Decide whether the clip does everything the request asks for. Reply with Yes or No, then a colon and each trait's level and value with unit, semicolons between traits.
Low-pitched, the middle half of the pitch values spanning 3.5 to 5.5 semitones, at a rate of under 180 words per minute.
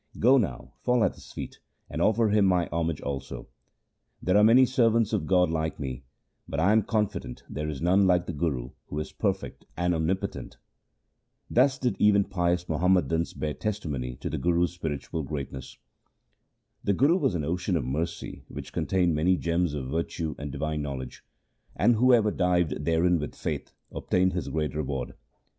Yes: very low, 85 Hz; average, 4.7 semitones; average, 170 wpm